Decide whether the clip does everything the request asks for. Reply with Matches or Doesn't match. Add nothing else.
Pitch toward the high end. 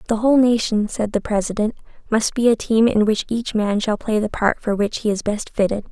Matches